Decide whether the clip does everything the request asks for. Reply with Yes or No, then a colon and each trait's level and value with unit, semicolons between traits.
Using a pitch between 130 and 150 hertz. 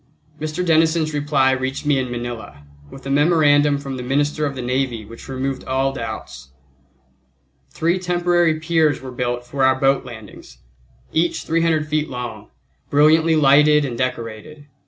Yes: medium, 140 Hz